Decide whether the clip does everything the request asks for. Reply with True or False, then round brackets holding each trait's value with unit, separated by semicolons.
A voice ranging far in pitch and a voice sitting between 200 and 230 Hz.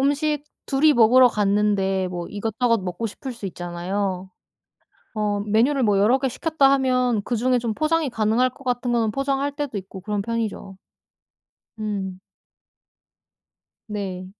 False (4.4 semitones; 225 Hz)